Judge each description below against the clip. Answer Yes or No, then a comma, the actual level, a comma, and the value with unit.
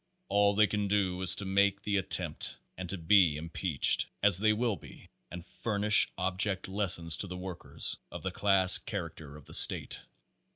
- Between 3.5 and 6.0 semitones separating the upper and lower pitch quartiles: No, narrow, 2.4 semitones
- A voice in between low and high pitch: No, very low, 95 Hz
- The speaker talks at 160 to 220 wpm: Yes, average, 175 wpm